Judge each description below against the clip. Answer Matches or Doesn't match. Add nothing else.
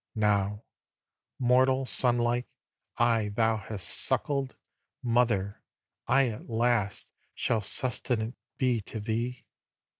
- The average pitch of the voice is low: Matches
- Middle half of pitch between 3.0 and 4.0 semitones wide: Doesn't match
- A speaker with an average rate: Doesn't match